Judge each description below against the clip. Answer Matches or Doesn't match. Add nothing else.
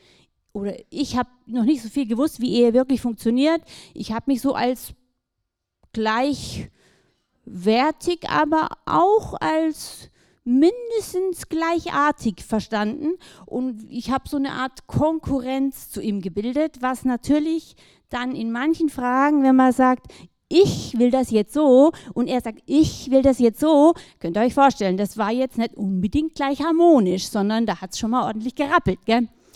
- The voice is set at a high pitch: Matches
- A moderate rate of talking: Matches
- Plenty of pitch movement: Doesn't match